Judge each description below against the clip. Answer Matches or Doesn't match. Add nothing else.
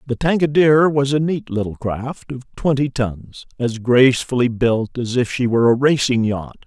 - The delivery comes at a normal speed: Matches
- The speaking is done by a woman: Doesn't match